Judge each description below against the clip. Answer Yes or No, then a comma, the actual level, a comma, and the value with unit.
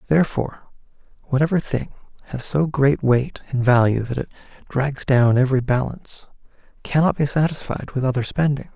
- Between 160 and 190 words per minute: No, average, 145 wpm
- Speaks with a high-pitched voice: No, low, 135 Hz